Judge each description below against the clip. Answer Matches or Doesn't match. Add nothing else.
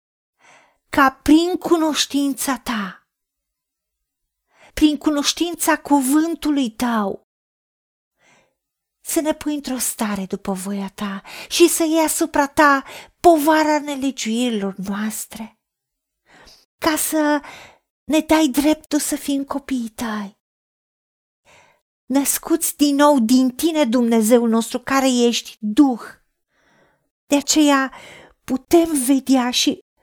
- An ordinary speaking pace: Doesn't match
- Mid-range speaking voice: Doesn't match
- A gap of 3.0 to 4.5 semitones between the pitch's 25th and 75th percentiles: Matches